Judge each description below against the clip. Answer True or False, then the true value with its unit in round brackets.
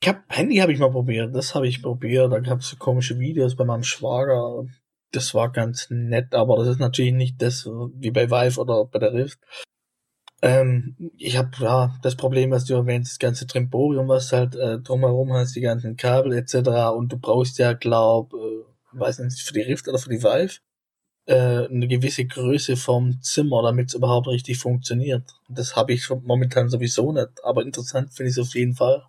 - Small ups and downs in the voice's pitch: True (1.2 semitones)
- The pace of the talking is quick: True (205 wpm)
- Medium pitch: False (125 Hz)